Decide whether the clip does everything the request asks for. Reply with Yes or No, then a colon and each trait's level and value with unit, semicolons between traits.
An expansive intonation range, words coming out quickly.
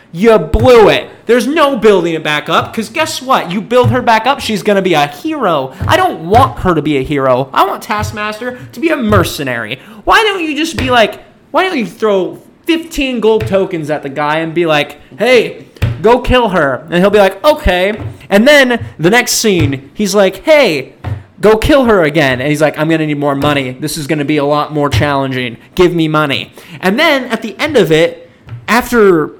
Yes: wide, 8.6 semitones; fast, 220 wpm